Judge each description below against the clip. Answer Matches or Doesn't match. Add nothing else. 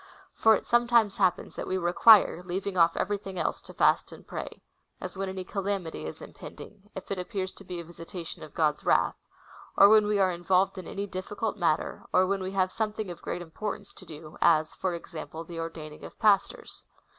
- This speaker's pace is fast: Matches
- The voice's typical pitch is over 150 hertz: Matches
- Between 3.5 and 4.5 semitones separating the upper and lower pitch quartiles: Doesn't match